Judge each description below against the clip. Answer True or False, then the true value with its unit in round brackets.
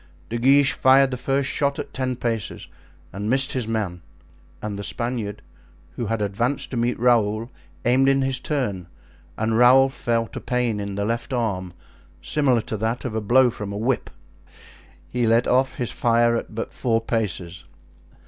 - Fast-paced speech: False (175 wpm)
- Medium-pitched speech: False (120 Hz)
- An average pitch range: True (3.2 semitones)